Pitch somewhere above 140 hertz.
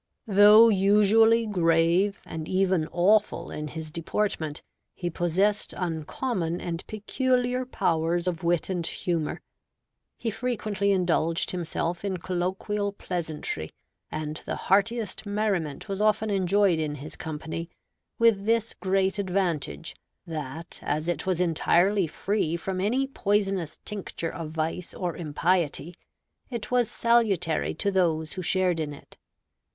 Yes: medium, 185 Hz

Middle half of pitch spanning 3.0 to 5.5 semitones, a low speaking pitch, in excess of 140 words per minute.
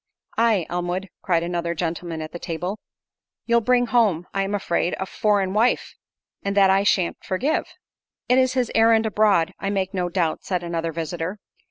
No: average, 3.8 semitones; high, 190 Hz; average, 170 wpm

